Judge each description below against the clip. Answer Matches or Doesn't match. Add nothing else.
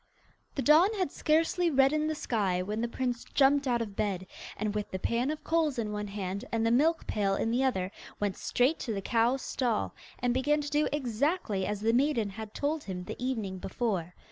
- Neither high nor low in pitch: Doesn't match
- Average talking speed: Doesn't match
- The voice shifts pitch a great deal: Matches